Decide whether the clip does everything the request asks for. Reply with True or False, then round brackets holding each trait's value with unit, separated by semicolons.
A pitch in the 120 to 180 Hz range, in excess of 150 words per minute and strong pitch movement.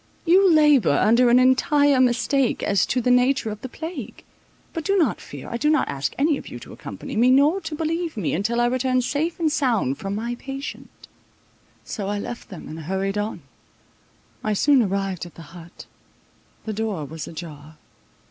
False (240 Hz; 185 wpm; 6.6 semitones)